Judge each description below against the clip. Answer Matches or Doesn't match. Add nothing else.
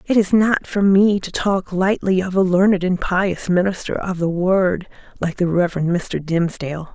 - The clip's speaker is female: Matches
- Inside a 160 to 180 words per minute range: Doesn't match